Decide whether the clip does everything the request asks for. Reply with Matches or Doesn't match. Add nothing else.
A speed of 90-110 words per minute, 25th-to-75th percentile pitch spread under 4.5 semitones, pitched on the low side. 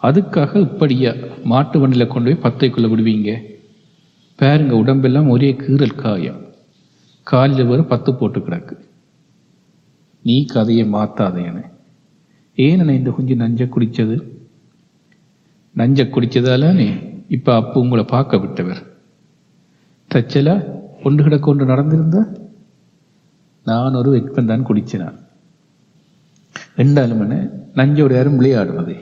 Matches